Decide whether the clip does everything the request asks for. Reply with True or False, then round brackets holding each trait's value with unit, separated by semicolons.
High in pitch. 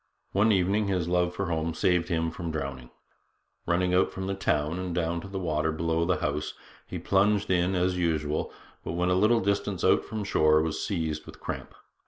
False (90 Hz)